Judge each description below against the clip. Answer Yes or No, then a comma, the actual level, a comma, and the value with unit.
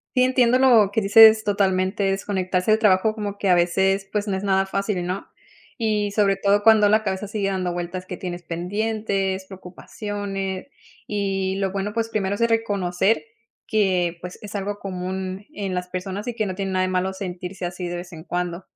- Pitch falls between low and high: No, high, 195 Hz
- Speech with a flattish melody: Yes, narrow, 2.0 semitones